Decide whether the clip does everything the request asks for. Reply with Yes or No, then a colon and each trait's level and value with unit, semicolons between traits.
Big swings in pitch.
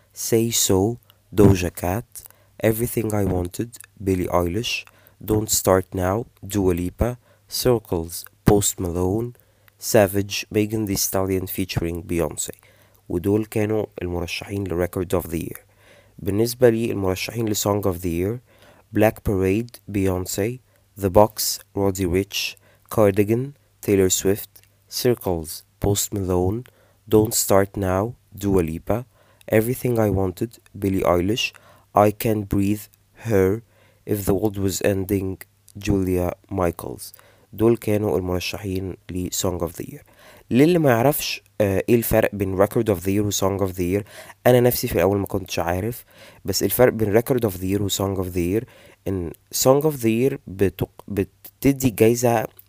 No: average, 2.7 semitones